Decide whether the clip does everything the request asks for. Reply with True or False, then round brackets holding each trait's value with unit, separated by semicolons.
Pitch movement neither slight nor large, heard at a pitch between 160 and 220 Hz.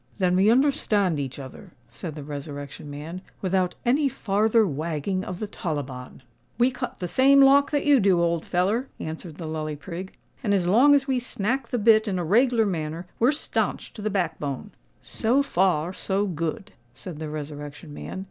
False (6.5 semitones; 185 Hz)